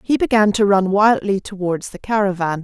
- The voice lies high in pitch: Yes, high, 200 Hz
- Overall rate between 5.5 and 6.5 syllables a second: No, 5.1 syllables/s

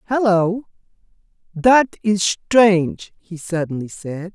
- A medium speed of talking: No, slow, 95 wpm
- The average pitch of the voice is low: No, high, 190 Hz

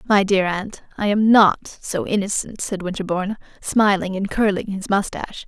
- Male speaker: No, female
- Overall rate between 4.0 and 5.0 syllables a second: Yes, 4.8 syllables/s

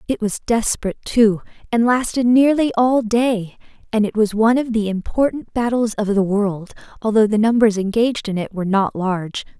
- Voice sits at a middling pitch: No, high, 220 Hz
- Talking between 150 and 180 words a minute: Yes, average, 175 wpm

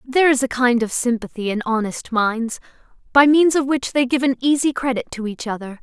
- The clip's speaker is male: No, female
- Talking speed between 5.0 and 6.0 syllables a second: Yes, 5.5 syllables/s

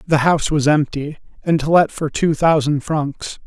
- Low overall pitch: No, medium, 150 Hz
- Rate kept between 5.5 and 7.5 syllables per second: No, 4.6 syllables/s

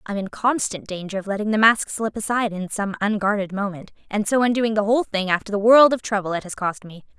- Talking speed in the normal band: No, fast, 240 wpm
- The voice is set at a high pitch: Yes, high, 210 Hz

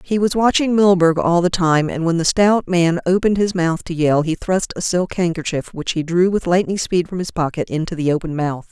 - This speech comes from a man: No, female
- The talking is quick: Yes, fast, 240 wpm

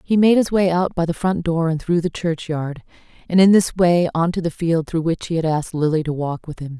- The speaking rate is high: Yes, fast, 275 wpm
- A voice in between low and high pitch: Yes, medium, 165 Hz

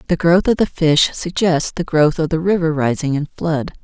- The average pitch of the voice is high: No, medium, 160 Hz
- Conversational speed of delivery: No, fast, 220 wpm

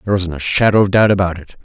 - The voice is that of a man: Yes, male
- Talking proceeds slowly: No, fast, 295 wpm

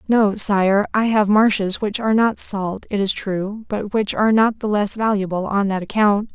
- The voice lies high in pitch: Yes, high, 205 Hz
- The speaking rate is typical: No, fast, 210 wpm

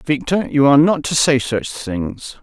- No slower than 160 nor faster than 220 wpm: Yes, average, 200 wpm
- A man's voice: Yes, male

